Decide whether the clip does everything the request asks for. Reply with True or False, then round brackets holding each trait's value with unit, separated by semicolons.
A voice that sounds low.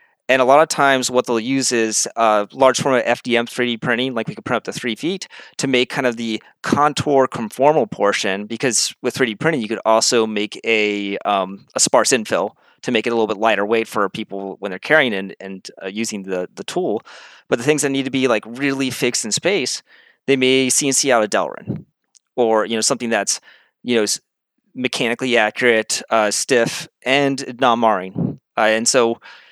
True (120 Hz)